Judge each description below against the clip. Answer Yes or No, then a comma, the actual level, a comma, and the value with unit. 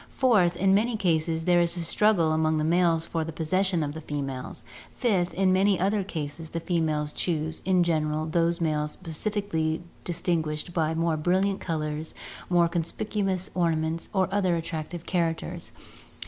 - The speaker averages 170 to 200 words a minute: No, average, 160 wpm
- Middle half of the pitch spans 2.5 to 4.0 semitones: Yes, average, 2.8 semitones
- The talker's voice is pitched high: No, medium, 170 Hz